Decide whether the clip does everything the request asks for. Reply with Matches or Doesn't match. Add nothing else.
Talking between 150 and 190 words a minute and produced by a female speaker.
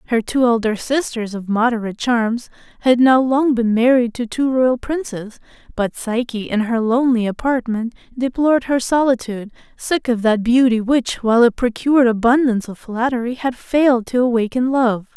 Matches